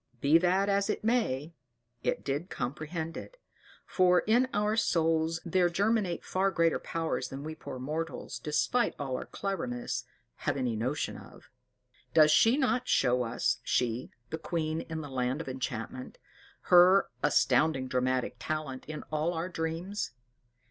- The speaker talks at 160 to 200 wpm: No, average, 150 wpm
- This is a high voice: No, medium, 160 Hz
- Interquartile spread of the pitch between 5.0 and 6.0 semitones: Yes, wide, 5.5 semitones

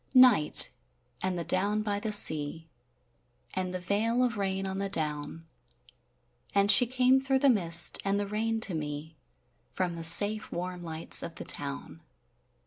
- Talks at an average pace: Yes, average, 160 wpm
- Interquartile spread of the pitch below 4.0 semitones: No, average, 4.4 semitones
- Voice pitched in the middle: No, high, 195 Hz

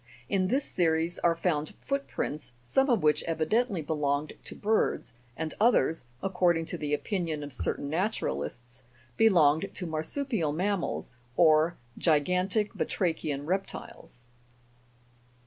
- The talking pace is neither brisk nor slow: No, slow, 130 wpm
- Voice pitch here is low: No, medium, 165 Hz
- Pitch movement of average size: Yes, average, 4.5 semitones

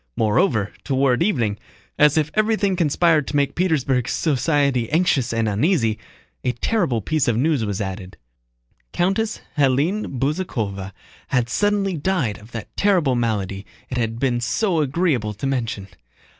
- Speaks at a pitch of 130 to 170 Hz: Yes, low, 135 Hz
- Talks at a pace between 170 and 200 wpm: No, average, 140 wpm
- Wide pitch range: Yes, wide, 6.7 semitones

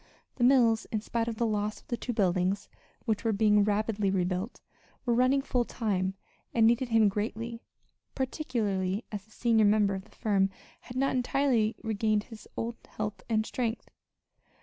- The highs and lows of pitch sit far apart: No, narrow, 2.5 semitones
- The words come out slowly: No, average, 170 wpm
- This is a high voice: Yes, high, 220 Hz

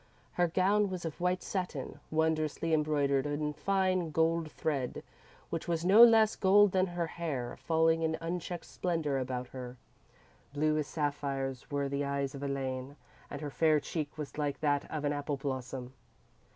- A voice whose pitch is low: No, medium, 155 Hz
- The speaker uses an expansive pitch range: No, average, 3.3 semitones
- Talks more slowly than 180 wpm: Yes, average, 165 wpm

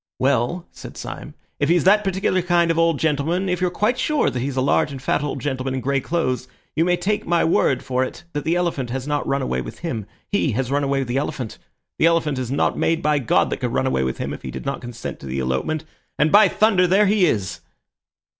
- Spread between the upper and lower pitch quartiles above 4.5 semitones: Yes, average, 5.3 semitones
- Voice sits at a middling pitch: Yes, medium, 145 Hz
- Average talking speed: No, fast, 250 wpm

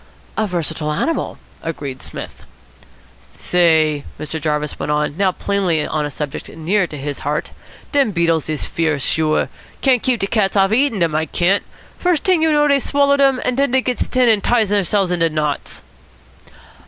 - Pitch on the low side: No, medium, 180 Hz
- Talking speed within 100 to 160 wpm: No, average, 180 wpm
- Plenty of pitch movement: Yes, wide, 8.0 semitones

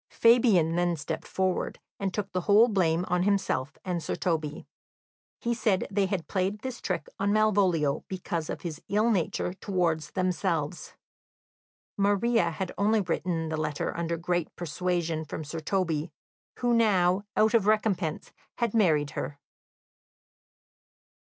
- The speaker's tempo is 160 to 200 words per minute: No, average, 140 wpm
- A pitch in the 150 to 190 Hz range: Yes, medium, 185 Hz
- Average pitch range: Yes, average, 3.7 semitones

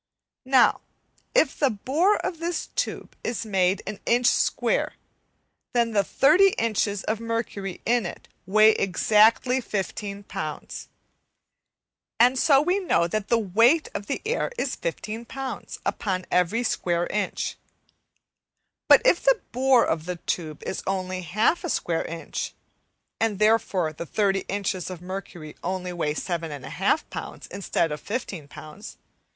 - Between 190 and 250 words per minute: No, average, 145 wpm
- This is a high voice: Yes, high, 210 Hz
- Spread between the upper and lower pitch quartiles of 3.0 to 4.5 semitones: No, average, 5.1 semitones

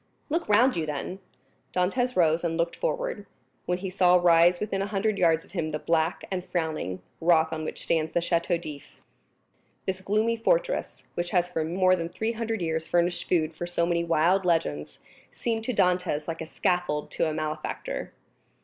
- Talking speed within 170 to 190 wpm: Yes, average, 185 wpm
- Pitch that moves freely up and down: No, average, 3.1 semitones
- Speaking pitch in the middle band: Yes, medium, 175 Hz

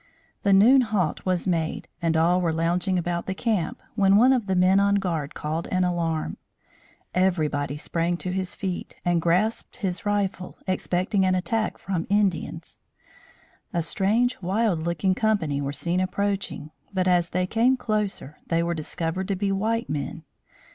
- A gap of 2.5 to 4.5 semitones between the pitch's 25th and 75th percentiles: Yes, average, 3.1 semitones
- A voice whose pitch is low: No, medium, 185 Hz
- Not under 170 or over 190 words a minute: No, average, 160 wpm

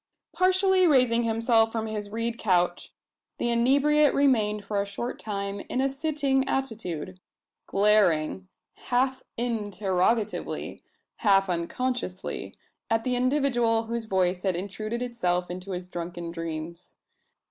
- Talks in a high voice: Yes, high, 220 Hz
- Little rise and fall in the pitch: No, average, 5.1 semitones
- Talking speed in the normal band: No, slow, 120 wpm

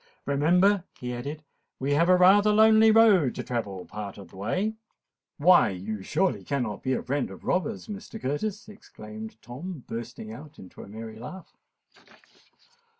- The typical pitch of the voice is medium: Yes, medium, 145 Hz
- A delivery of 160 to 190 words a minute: No, average, 150 wpm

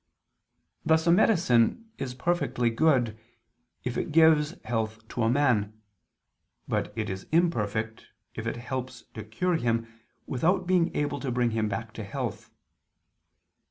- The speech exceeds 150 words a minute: No, average, 140 wpm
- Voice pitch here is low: Yes, low, 125 Hz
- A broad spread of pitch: Yes, wide, 6.2 semitones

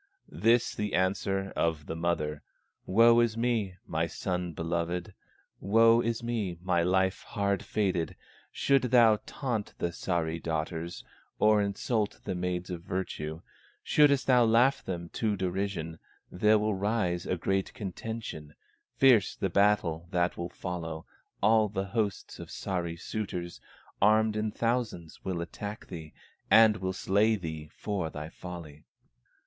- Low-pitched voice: Yes, very low, 95 Hz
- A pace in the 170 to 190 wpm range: No, average, 140 wpm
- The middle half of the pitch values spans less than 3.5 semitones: No, average, 4.1 semitones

